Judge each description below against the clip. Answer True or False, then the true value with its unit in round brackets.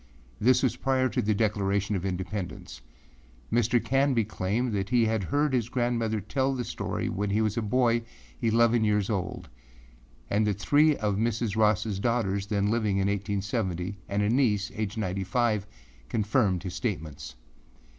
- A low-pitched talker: True (105 Hz)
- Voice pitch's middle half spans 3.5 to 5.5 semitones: False (3.1 semitones)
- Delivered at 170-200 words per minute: False (160 wpm)